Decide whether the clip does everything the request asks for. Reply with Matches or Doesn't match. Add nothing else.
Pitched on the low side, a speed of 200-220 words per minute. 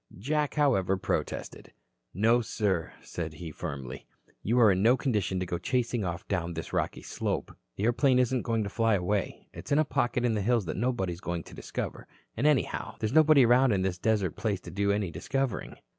Matches